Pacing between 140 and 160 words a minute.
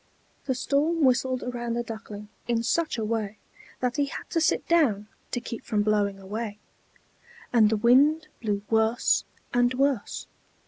Yes: average, 155 wpm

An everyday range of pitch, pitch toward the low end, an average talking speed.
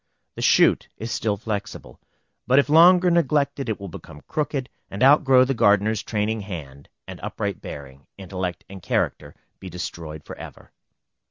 No: wide, 7.2 semitones; low, 105 Hz; average, 150 wpm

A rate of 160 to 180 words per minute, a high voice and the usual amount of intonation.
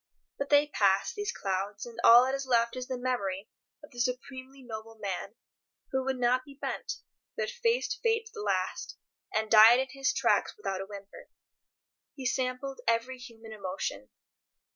Yes: average, 170 wpm; very high, 250 Hz; average, 3.8 semitones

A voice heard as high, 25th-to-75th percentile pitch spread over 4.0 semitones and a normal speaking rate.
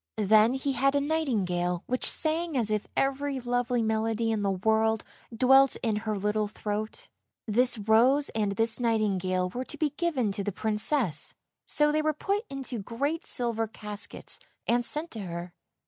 Yes: high, 225 Hz; average, 4.5 semitones; average, 165 wpm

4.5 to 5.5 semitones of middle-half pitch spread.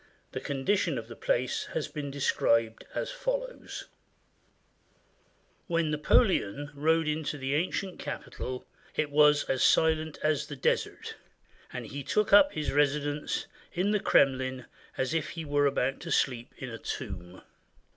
No: average, 3.6 semitones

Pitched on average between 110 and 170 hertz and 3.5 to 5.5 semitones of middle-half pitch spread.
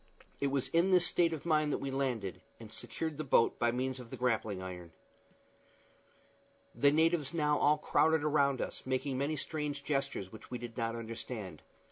Yes: low, 135 Hz; average, 4.4 semitones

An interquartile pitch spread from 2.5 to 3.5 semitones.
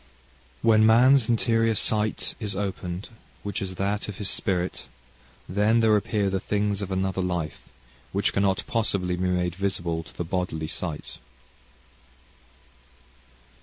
Yes: average, 2.8 semitones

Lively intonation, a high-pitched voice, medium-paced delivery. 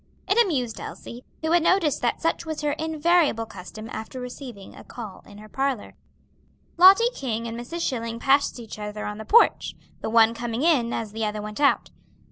Yes: wide, 6.1 semitones; high, 245 Hz; average, 190 wpm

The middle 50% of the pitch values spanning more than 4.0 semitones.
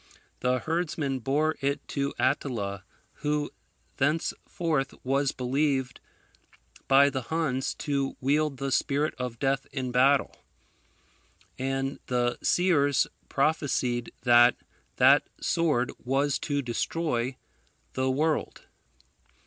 No: narrow, 2.6 semitones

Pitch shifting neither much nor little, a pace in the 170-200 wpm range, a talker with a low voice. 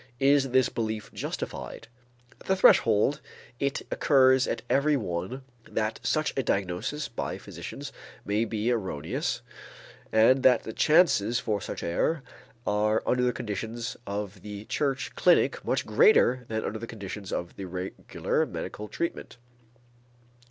No: average, 4.3 semitones; average, 140 wpm; low, 115 Hz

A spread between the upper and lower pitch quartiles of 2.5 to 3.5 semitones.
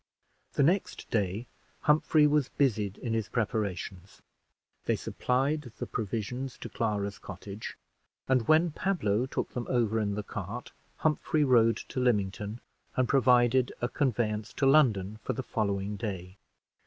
No: average, 4.4 semitones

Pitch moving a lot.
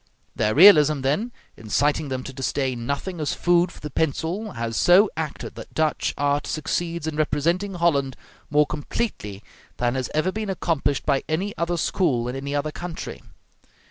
No: average, 4.2 semitones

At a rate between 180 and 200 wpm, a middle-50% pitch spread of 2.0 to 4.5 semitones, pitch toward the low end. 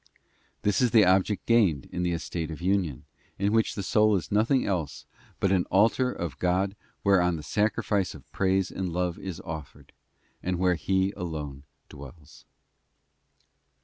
No: average, 155 wpm; average, 3.3 semitones; very low, 90 Hz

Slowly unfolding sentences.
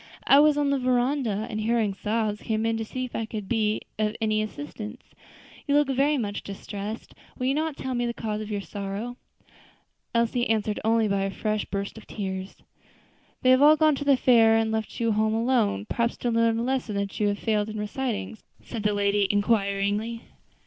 No: fast, 205 wpm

